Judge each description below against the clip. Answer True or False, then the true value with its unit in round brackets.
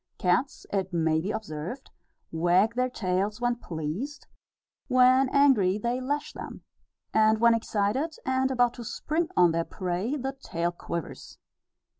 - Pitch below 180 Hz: False (220 Hz)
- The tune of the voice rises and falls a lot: True (6.3 semitones)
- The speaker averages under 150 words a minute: True (140 wpm)